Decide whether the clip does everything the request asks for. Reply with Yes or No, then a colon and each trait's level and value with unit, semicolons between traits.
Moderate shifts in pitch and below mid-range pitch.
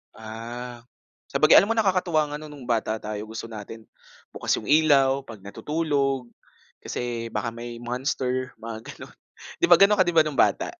Yes: average, 4.8 semitones; low, 125 Hz